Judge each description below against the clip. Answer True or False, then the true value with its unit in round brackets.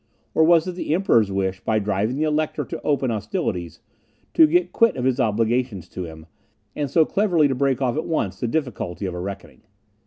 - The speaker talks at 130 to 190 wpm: False (205 wpm)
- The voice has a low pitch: True (125 Hz)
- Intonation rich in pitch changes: True (7.8 semitones)